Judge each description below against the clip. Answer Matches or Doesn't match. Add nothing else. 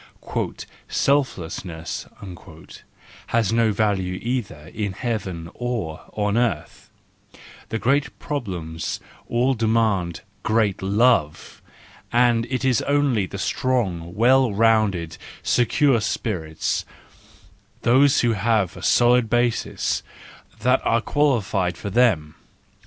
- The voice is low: Matches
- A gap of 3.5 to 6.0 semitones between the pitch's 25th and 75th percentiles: Matches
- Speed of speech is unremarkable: Doesn't match